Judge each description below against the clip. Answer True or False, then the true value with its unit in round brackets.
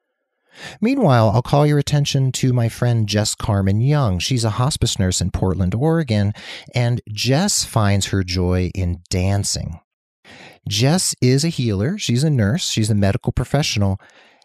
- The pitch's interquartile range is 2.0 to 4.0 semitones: False (5.3 semitones)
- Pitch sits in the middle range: False (115 Hz)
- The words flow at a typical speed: True (150 wpm)